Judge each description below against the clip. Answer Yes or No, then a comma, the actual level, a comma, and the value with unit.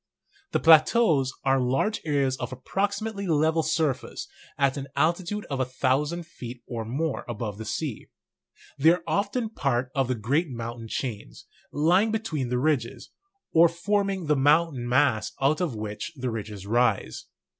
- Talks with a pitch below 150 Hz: Yes, medium, 140 Hz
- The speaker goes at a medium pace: Yes, average, 155 wpm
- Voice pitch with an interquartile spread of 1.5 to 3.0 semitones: No, wide, 5.4 semitones